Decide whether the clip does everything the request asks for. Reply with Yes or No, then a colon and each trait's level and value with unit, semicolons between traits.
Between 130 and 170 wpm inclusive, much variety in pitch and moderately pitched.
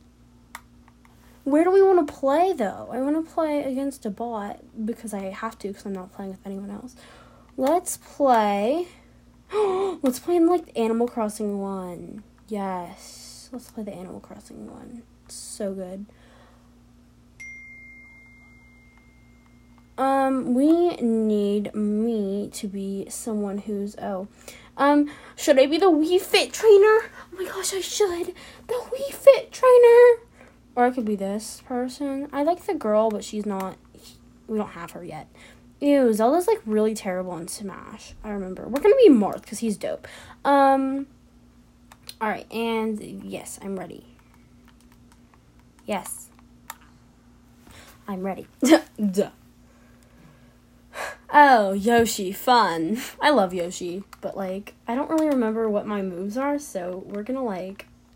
No: average, 140 wpm; wide, 6.6 semitones; high, 220 Hz